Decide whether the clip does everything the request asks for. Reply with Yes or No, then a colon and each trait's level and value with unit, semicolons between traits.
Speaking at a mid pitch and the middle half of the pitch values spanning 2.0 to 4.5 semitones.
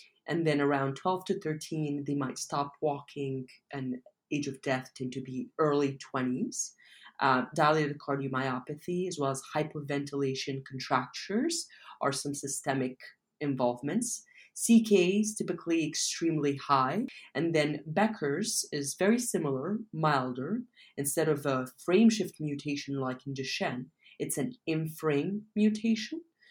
No: medium, 150 Hz; average, 5.2 semitones